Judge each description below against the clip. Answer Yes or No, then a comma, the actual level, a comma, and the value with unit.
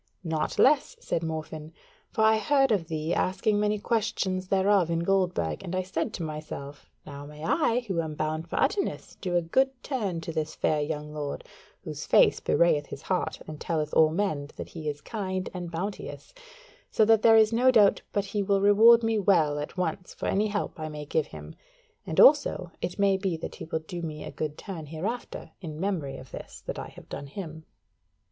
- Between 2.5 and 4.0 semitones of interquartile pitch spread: No, average, 4.8 semitones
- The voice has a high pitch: No, medium, 175 Hz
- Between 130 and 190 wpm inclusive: No, fast, 205 wpm